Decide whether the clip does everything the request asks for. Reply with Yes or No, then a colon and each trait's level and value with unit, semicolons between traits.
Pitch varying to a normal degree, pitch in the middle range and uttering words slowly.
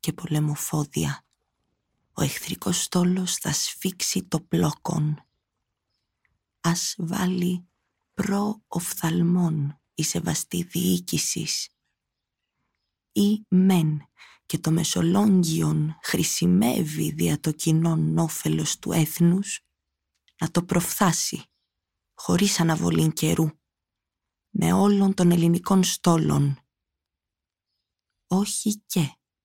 Yes: average, 3.9 semitones; medium, 165 Hz; slow, 80 wpm